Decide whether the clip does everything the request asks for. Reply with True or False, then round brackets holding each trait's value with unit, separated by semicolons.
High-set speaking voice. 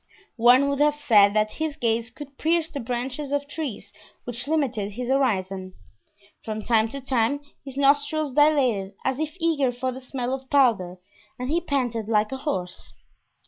True (255 Hz)